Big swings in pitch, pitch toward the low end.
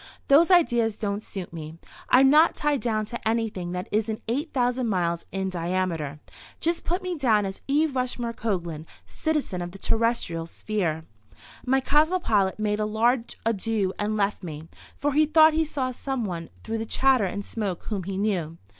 No: wide, 5.9 semitones; high, 220 Hz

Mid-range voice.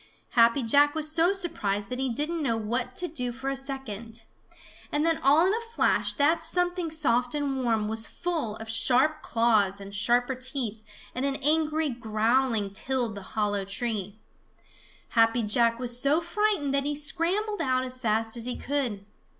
No: very high, 255 Hz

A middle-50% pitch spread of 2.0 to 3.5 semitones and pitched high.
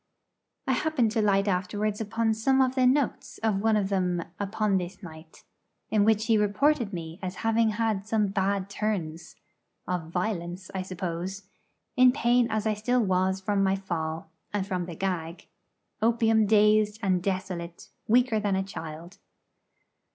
Yes: average, 3.2 semitones; high, 200 Hz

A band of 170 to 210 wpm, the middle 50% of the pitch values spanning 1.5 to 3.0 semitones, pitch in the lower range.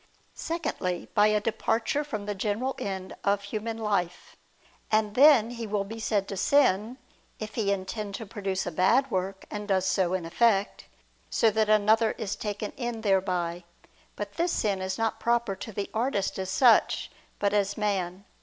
No: average, 175 wpm; average, 2.7 semitones; high, 205 Hz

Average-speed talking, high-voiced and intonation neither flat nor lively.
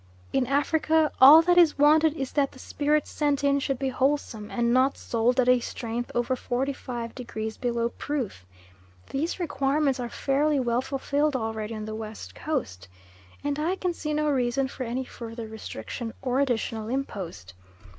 Yes: average, 165 wpm; very high, 260 Hz; average, 3.7 semitones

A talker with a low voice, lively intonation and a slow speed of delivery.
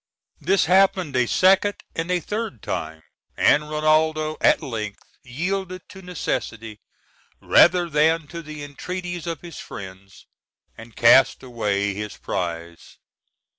No: medium, 155 Hz; wide, 8.0 semitones; slow, 125 wpm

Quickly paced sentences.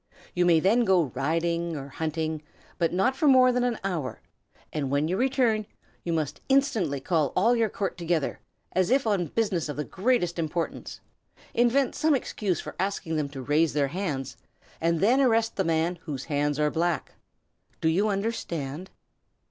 No: average, 170 wpm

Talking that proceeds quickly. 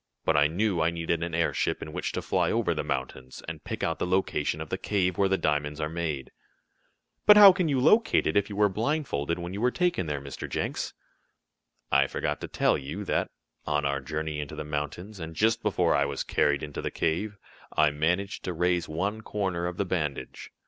Yes: fast, 215 wpm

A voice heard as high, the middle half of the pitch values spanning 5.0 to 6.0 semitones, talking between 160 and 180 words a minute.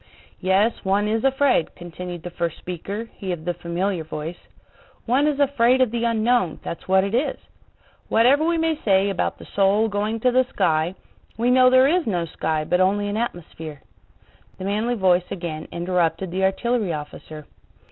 Yes: high, 195 Hz; wide, 5.4 semitones; average, 175 wpm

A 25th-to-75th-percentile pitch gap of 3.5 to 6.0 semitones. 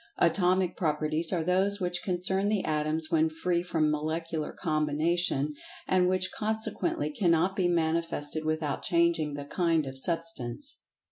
No: average, 2.8 semitones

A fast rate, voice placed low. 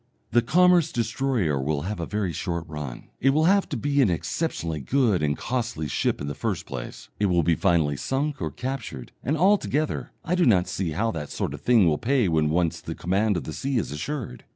Yes: fast, 220 wpm; low, 105 Hz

